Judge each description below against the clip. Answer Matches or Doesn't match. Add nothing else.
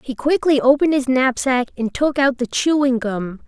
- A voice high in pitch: Matches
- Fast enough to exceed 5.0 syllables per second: Doesn't match